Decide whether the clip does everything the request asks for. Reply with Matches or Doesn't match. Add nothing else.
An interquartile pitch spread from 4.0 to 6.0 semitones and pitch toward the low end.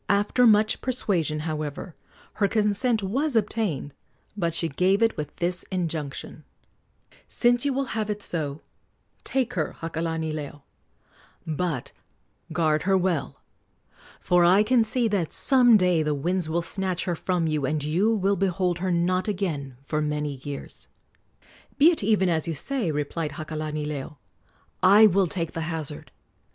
Doesn't match